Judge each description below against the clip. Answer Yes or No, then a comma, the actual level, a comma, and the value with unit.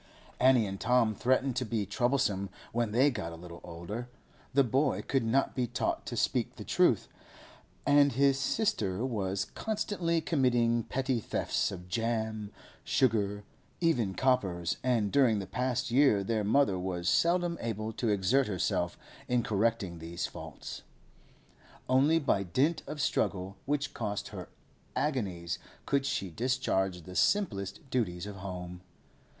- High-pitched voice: No, low, 115 Hz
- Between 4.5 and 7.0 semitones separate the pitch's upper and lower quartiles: Yes, wide, 5.4 semitones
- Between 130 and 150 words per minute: Yes, average, 145 wpm